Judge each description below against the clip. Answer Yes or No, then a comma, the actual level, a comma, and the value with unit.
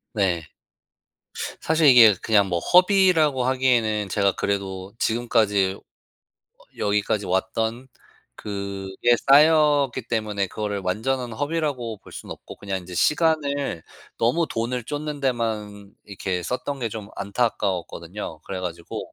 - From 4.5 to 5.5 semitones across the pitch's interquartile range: Yes, average, 5.1 semitones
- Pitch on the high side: No, low, 110 Hz